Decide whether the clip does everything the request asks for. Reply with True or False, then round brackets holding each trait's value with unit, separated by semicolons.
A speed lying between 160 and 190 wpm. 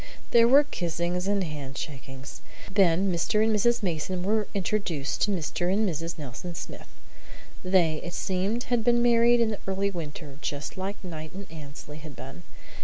True (165 wpm)